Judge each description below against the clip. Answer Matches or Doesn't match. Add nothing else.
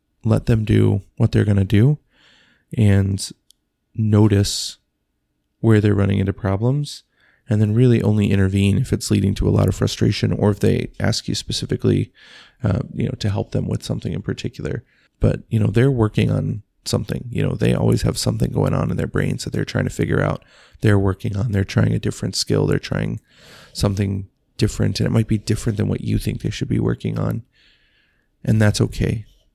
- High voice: Doesn't match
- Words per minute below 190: Doesn't match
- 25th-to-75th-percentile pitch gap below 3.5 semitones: Matches